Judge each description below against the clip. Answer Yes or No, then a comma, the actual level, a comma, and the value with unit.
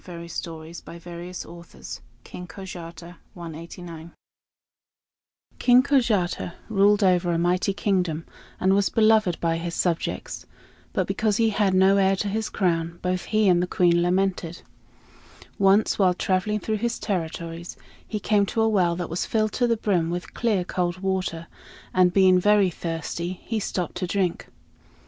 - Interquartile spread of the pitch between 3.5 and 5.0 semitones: No, average, 3.0 semitones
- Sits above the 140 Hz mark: Yes, medium, 185 Hz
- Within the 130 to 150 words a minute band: Yes, average, 145 wpm